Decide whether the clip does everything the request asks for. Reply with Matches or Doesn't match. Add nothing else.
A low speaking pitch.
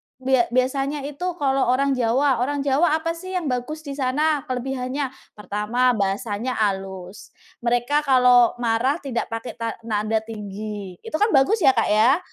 Doesn't match